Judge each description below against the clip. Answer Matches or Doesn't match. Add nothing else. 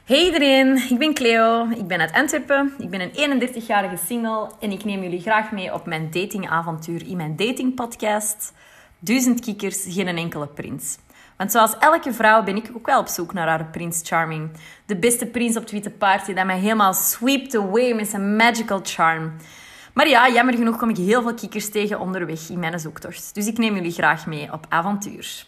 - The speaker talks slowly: Doesn't match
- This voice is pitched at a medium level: Doesn't match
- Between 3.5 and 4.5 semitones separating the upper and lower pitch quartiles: Doesn't match